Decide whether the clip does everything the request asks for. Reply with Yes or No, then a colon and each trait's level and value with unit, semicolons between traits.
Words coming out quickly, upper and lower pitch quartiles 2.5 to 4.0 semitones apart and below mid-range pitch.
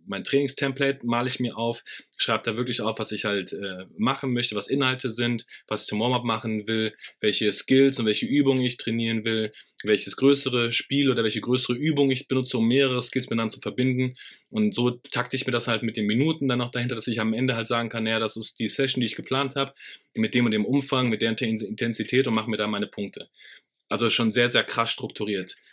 Yes: fast, 225 wpm; average, 2.9 semitones; low, 120 Hz